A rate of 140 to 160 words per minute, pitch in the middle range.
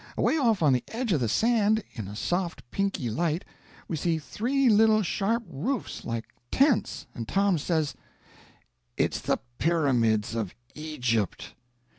Yes: average, 145 wpm; medium, 170 Hz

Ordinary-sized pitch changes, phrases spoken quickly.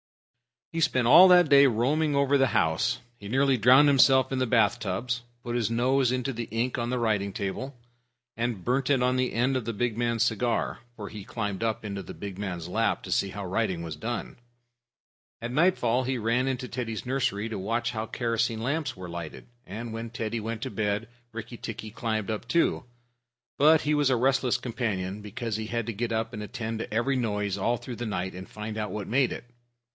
Yes: average, 3.1 semitones; fast, 210 wpm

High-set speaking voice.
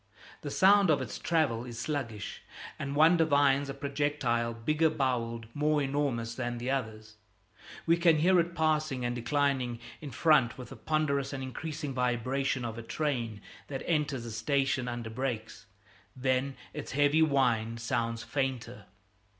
No: low, 135 Hz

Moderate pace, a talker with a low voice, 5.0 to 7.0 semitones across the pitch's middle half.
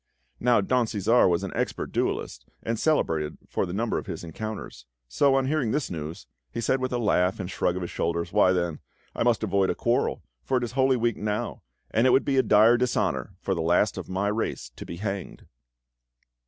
No: fast, 215 wpm; low, 105 Hz; wide, 5.5 semitones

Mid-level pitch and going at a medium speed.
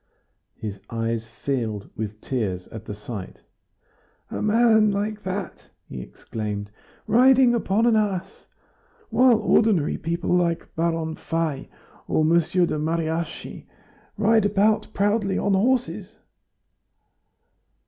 No: medium, 170 Hz; slow, 110 wpm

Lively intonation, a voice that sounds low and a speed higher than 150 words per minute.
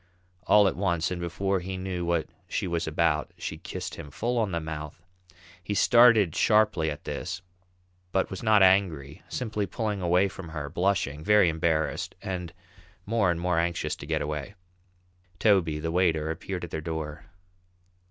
No: average, 3.6 semitones; very low, 85 Hz; average, 165 wpm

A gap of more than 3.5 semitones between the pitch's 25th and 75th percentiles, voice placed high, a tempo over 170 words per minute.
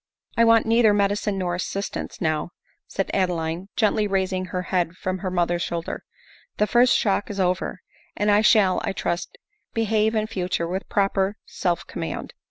No: average, 2.7 semitones; high, 195 Hz; average, 180 wpm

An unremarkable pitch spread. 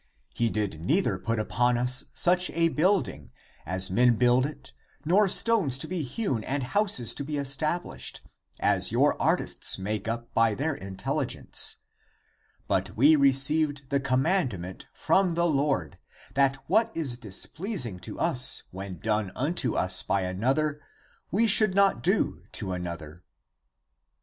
No: wide, 7.3 semitones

